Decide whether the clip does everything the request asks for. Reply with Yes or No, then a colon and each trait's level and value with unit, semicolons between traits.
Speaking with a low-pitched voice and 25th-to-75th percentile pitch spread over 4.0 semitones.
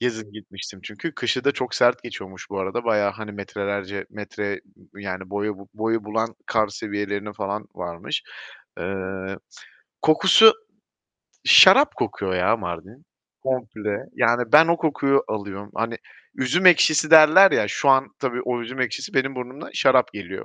Yes: low, 110 Hz; average, 4.4 semitones